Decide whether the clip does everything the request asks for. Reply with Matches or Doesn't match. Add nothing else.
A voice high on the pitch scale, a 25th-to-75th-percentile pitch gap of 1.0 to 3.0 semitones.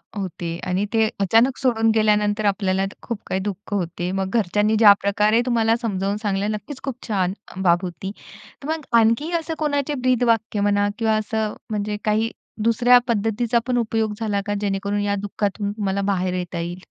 Matches